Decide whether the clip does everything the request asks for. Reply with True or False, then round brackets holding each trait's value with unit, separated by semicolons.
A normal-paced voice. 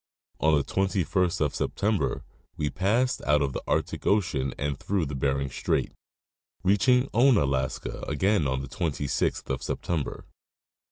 False (130 wpm)